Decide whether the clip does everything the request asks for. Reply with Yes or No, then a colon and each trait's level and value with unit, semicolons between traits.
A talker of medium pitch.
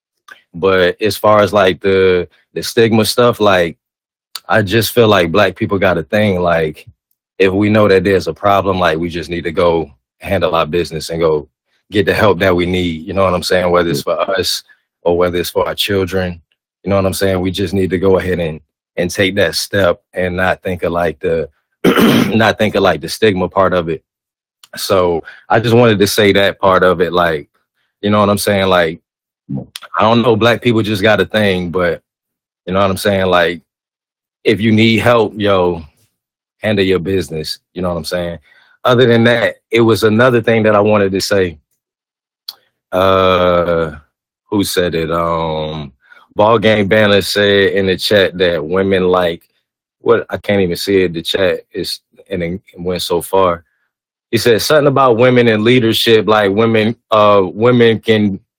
No: very low, 95 Hz